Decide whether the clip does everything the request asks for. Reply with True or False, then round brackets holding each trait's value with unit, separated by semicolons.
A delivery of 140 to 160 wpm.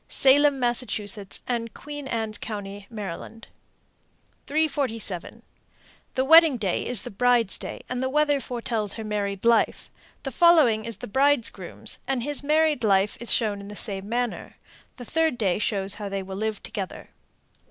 True (155 wpm)